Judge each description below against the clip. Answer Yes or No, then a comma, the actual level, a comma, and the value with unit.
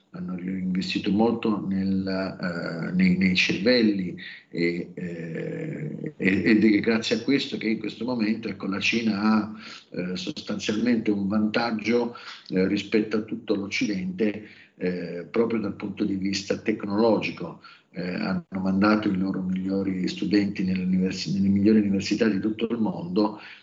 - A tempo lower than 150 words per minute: Yes, average, 135 wpm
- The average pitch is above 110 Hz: No, low, 105 Hz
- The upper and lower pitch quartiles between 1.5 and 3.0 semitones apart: Yes, narrow, 2.6 semitones